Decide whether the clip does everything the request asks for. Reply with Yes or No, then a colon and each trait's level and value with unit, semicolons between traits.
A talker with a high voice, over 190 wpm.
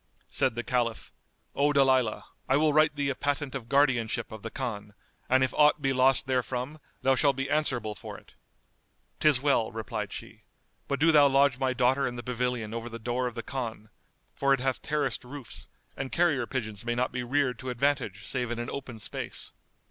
No: low, 130 Hz; average, 200 wpm